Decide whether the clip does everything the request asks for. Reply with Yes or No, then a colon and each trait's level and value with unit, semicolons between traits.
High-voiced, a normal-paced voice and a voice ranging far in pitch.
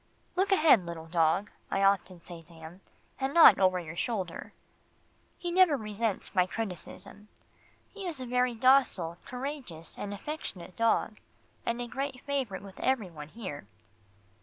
Yes: high, 210 Hz; average, 150 wpm; wide, 6.9 semitones